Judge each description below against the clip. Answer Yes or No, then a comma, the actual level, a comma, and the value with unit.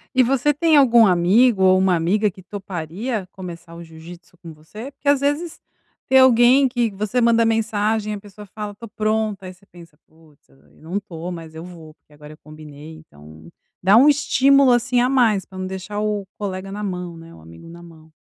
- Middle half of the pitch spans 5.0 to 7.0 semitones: Yes, wide, 5.5 semitones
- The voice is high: Yes, high, 195 Hz